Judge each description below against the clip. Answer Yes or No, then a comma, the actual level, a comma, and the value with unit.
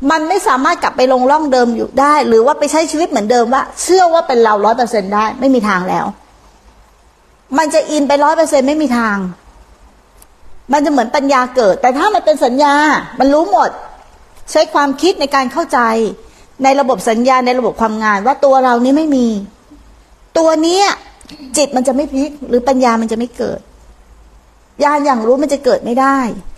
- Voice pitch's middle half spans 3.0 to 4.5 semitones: Yes, average, 3.5 semitones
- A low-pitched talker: No, very high, 270 Hz